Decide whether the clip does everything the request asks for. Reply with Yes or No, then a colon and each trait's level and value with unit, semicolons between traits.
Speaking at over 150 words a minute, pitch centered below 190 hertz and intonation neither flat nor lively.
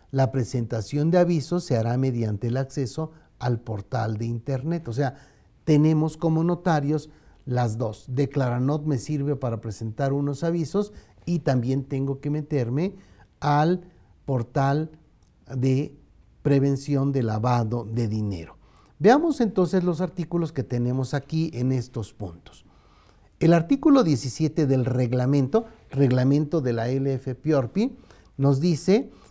No: slow, 125 wpm; medium, 140 Hz; average, 4.3 semitones